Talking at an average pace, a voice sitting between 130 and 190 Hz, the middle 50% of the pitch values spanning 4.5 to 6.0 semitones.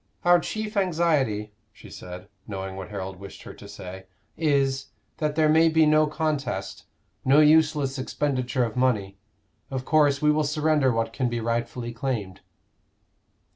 Yes: average, 150 wpm; low, 135 Hz; average, 5.3 semitones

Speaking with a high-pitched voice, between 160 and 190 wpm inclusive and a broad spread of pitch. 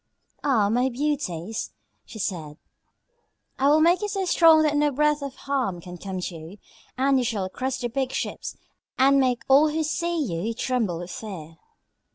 Yes: very high, 255 Hz; average, 180 wpm; wide, 7.3 semitones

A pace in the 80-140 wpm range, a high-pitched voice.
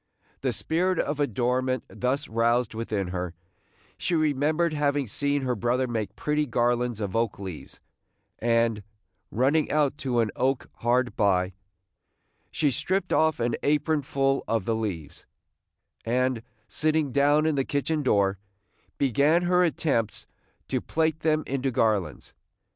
No: slow, 135 wpm; low, 130 Hz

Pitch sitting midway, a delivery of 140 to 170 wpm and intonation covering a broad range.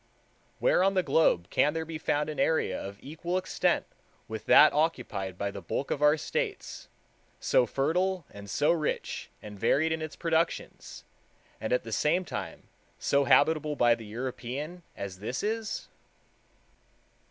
Yes: medium, 150 Hz; average, 155 wpm; wide, 6.2 semitones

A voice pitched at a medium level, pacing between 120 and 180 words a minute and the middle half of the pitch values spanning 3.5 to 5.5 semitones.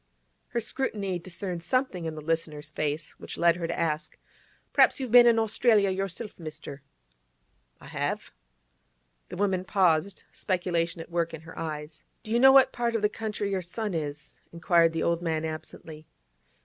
Yes: medium, 175 Hz; average, 175 wpm; average, 4.5 semitones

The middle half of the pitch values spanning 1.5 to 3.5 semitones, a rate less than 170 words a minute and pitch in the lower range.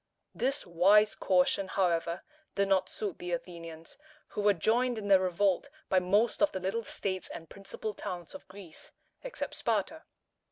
No: average, 2.8 semitones; average, 160 wpm; high, 190 Hz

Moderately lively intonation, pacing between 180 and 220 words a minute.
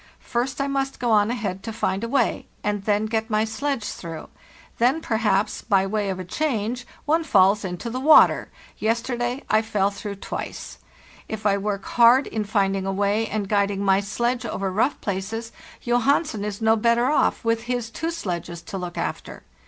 Yes: average, 3.3 semitones; average, 185 wpm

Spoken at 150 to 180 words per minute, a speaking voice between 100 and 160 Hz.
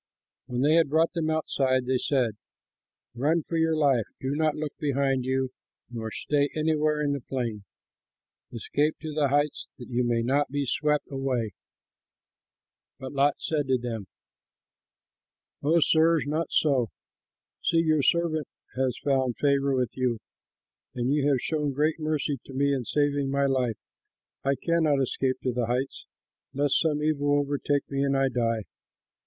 Yes: average, 160 wpm; medium, 140 Hz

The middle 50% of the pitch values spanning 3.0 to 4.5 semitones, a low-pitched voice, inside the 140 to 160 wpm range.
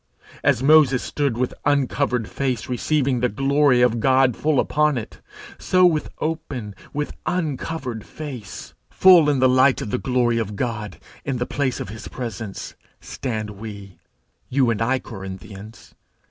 Yes: average, 4.1 semitones; low, 125 Hz; average, 150 wpm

